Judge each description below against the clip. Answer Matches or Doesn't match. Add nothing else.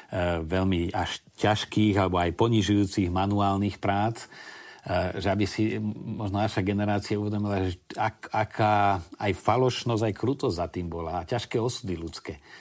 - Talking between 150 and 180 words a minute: Doesn't match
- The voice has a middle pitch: Doesn't match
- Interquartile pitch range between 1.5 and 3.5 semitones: Matches